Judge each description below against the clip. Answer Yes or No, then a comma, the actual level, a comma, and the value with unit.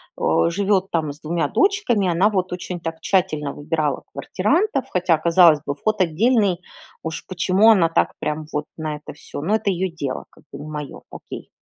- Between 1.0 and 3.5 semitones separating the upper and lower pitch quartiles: No, average, 4.4 semitones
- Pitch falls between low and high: Yes, medium, 175 Hz